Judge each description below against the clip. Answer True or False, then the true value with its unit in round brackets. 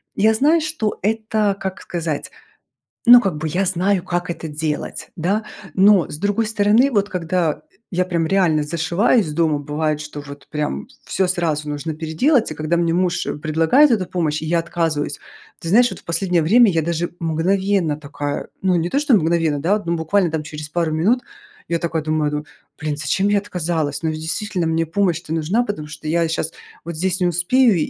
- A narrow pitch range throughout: False (4.0 semitones)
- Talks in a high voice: False (170 Hz)